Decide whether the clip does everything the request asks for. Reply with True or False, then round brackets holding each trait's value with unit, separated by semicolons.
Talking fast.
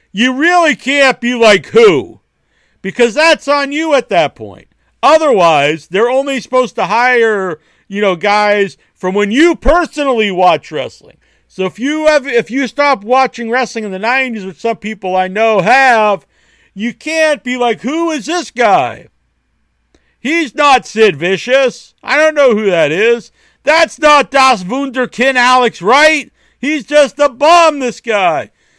False (160 wpm)